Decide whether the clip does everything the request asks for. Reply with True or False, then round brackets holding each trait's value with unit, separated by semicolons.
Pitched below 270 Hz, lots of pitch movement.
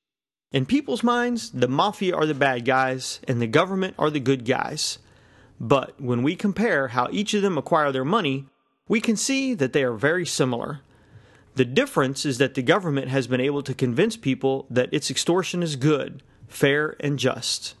False (140 Hz; 4.3 semitones)